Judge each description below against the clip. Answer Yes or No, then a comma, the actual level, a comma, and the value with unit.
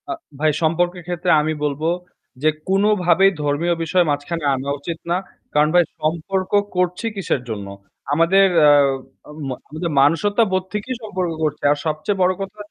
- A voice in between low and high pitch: Yes, medium, 175 Hz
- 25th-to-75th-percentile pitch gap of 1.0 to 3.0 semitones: No, average, 3.6 semitones